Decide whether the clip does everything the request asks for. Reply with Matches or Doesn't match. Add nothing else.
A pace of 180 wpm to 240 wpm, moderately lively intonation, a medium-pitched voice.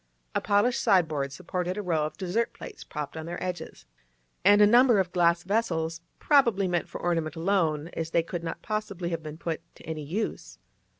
Matches